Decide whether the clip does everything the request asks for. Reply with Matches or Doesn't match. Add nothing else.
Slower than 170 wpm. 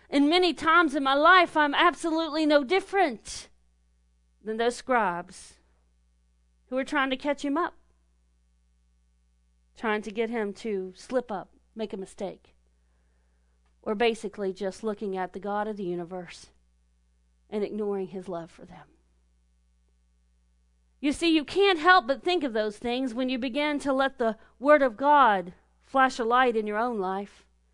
Matches